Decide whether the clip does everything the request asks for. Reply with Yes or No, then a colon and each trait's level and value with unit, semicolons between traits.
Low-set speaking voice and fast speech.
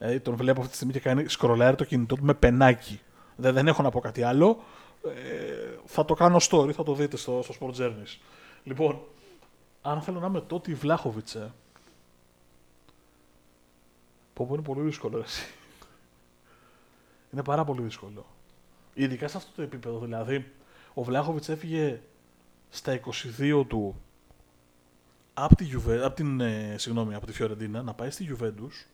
No: low, 125 Hz; average, 150 wpm